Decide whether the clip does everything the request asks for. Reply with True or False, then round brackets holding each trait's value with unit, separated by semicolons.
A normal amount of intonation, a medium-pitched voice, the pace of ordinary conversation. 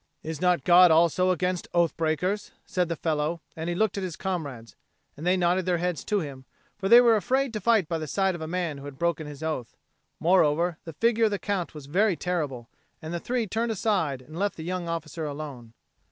False (3.4 semitones; 170 Hz; 225 wpm)